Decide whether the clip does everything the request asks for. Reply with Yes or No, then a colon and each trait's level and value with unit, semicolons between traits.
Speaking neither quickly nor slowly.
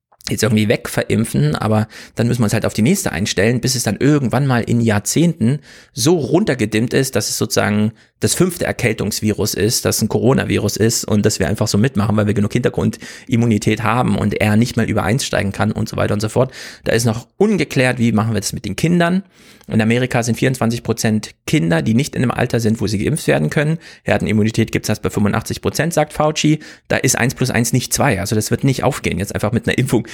No: fast, 225 wpm